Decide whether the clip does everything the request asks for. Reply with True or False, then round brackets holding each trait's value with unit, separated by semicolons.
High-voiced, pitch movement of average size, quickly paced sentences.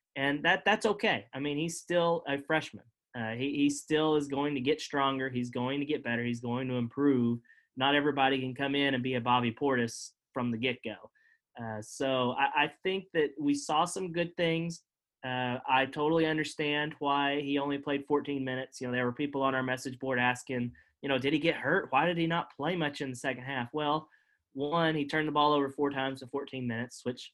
False (140 Hz; 3.1 semitones; 225 wpm)